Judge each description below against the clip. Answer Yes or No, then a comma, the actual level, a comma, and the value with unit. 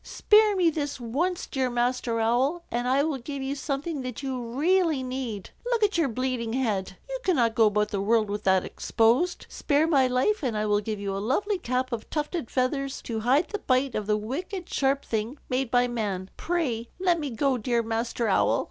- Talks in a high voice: Yes, very high, 255 Hz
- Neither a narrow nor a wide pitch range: Yes, average, 4.7 semitones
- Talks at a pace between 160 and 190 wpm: No, fast, 205 wpm